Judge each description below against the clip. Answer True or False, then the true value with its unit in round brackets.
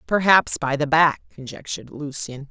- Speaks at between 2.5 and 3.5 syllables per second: False (4.9 syllables/s)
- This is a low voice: False (150 Hz)